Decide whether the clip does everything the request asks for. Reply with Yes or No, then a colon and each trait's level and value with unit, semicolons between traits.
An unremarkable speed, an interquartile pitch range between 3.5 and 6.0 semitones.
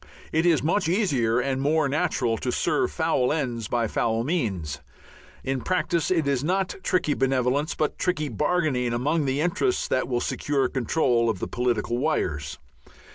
Yes: average, 160 wpm; average, 4.9 semitones